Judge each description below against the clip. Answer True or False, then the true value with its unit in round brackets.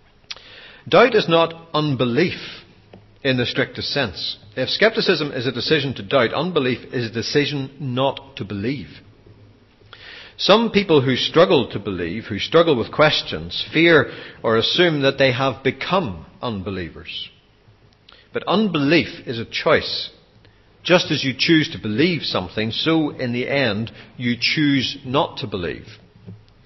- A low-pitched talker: True (130 Hz)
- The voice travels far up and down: True (5.9 semitones)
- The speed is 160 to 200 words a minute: False (135 wpm)